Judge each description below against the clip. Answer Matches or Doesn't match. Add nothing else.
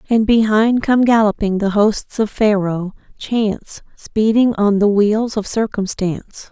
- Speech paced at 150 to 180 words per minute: Doesn't match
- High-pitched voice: Matches